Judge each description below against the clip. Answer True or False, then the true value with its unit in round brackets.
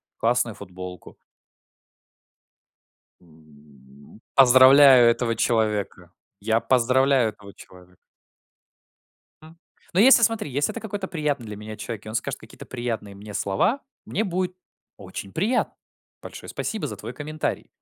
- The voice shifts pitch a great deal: True (6.5 semitones)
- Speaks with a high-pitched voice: False (115 Hz)